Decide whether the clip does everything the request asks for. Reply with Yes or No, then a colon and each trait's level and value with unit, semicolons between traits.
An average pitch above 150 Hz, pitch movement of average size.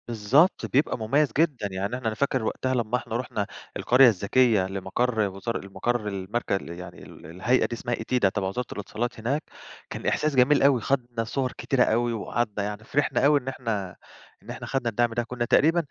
No: low, 120 Hz; average, 3.7 semitones